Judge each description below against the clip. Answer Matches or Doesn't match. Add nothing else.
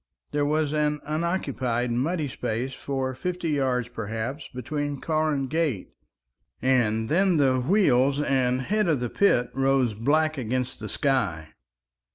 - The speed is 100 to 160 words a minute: Matches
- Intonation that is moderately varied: Matches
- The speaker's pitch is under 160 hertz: Matches